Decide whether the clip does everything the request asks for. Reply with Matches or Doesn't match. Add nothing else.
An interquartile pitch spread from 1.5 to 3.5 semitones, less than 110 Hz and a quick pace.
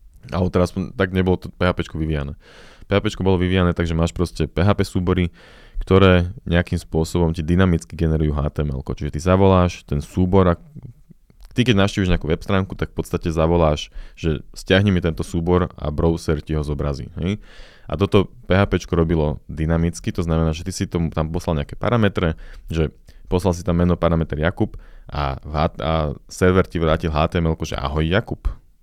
Matches